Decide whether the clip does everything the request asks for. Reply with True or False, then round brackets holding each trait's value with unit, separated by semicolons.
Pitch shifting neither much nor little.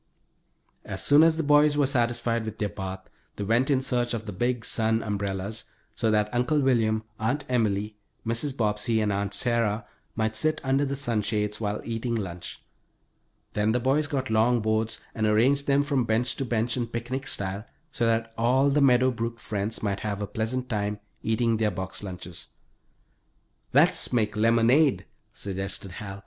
True (3.2 semitones)